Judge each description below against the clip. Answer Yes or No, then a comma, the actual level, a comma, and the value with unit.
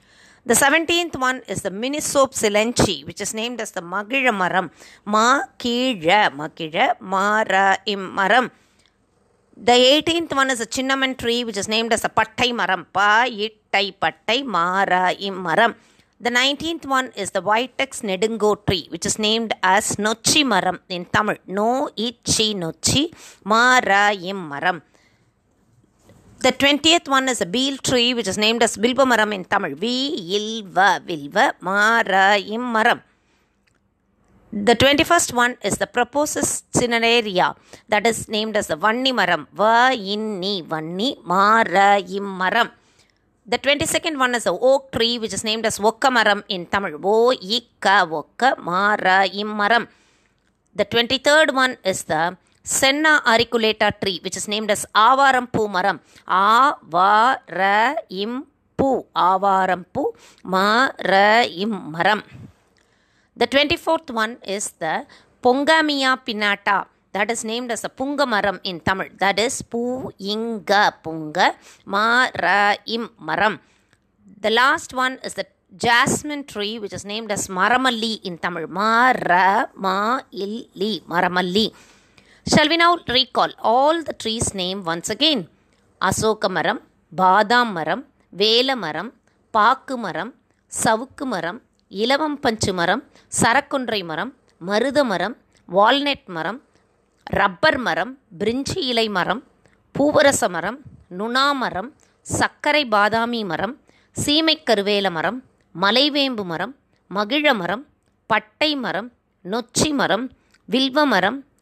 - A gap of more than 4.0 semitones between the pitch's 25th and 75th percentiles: Yes, average, 4.7 semitones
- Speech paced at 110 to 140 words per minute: Yes, average, 120 wpm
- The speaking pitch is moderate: No, high, 220 Hz